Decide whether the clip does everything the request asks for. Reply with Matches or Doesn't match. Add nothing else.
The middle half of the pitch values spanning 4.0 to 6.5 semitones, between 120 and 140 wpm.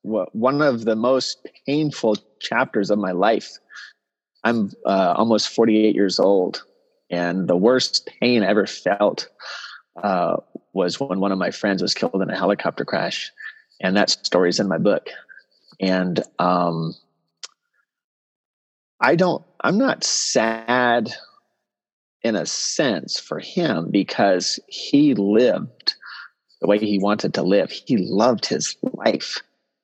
Matches